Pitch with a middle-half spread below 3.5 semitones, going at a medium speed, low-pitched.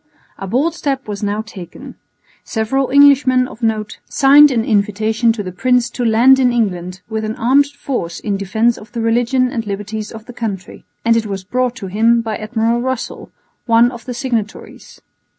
No: average, 3.1 semitones; average, 185 wpm; high, 230 Hz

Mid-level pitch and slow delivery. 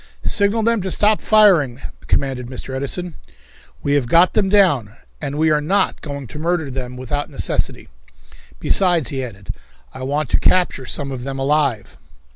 No: medium, 145 Hz; average, 165 wpm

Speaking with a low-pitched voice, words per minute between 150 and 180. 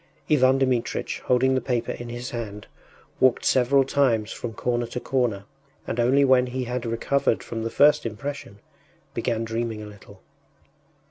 Yes: low, 120 Hz; average, 155 wpm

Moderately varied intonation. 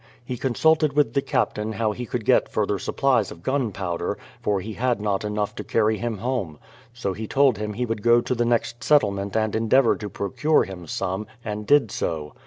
Yes: average, 3.3 semitones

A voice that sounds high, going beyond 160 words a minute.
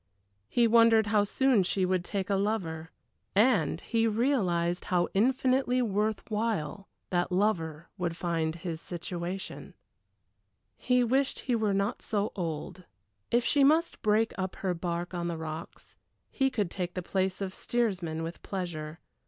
No: high, 195 Hz; average, 150 wpm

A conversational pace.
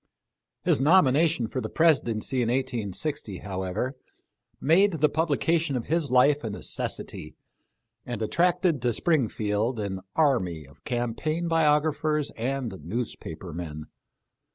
No: slow, 125 wpm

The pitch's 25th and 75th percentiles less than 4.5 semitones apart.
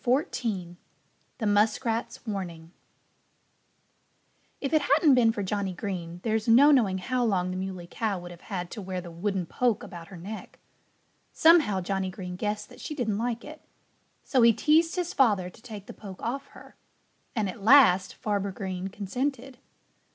No: average, 4.8 semitones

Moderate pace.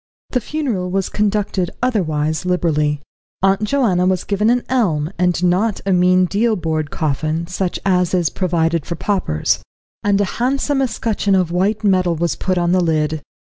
Yes: average, 165 wpm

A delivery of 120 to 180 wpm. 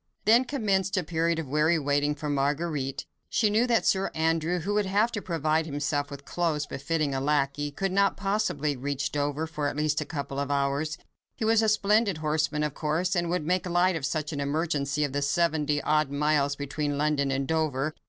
No: average, 195 wpm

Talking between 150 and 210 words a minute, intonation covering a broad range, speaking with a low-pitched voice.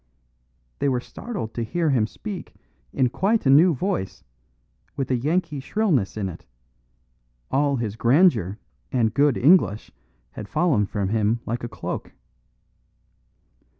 No: slow, 135 wpm; wide, 6.8 semitones; low, 130 Hz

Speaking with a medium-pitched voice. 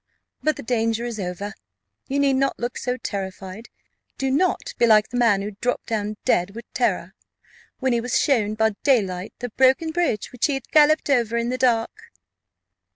No: high, 235 Hz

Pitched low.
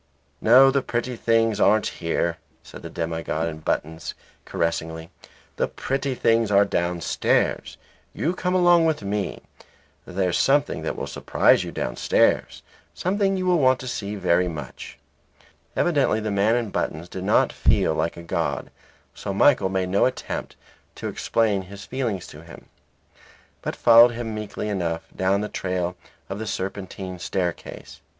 Yes: low, 100 Hz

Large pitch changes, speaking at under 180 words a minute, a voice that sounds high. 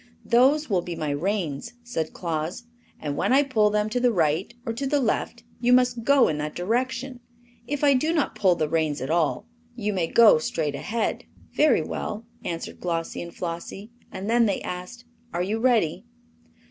No: wide, 6.8 semitones; average, 185 wpm; high, 210 Hz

